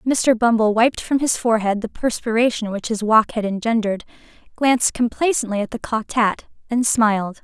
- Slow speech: No, average, 170 wpm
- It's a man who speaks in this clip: No, female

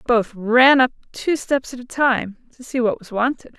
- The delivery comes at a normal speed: No, fast, 220 wpm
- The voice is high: Yes, high, 245 Hz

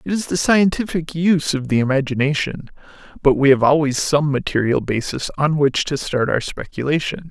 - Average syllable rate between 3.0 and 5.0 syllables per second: No, 5.3 syllables/s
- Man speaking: Yes, male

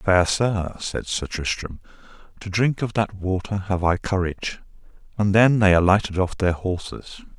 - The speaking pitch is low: Yes, very low, 95 Hz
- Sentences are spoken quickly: No, average, 165 wpm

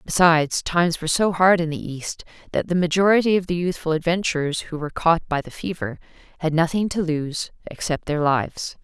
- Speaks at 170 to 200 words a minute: Yes, average, 190 wpm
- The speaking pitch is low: No, medium, 170 Hz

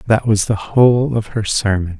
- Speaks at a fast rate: Yes, fast, 210 wpm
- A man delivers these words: Yes, male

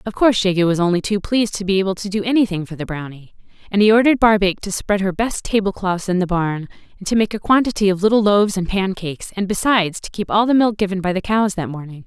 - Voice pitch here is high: Yes, high, 195 Hz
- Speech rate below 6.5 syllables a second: No, 6.6 syllables/s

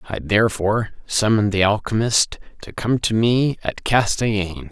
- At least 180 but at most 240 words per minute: No, average, 140 wpm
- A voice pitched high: No, low, 105 Hz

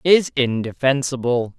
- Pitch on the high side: No, low, 130 Hz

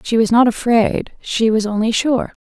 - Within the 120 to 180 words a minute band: No, average, 200 wpm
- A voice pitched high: Yes, high, 230 Hz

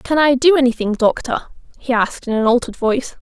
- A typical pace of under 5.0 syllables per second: No, 6.3 syllables/s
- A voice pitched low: No, very high, 255 Hz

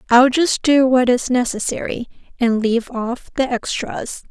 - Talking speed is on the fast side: No, average, 155 wpm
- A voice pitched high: Yes, high, 245 Hz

